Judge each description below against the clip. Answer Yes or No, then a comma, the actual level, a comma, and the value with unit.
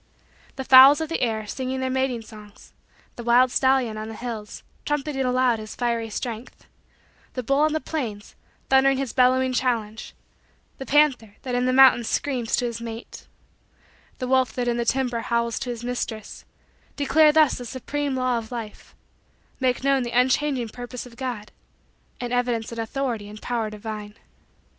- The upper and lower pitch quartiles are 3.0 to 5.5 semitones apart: No, narrow, 2.5 semitones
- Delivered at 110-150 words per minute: No, average, 170 wpm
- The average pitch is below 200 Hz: No, high, 245 Hz